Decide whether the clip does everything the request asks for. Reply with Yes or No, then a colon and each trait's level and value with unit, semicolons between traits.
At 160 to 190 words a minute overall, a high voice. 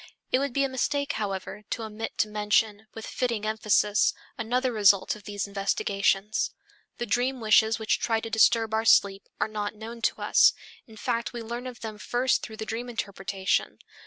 Yes: average, 185 wpm; high, 220 Hz